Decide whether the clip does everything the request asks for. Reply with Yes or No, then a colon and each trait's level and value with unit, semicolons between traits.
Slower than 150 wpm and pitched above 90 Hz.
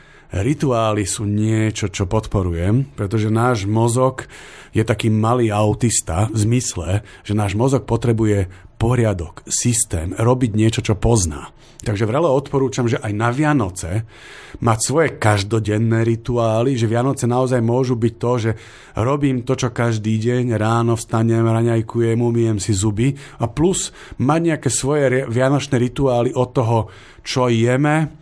Yes: average, 135 wpm; low, 115 Hz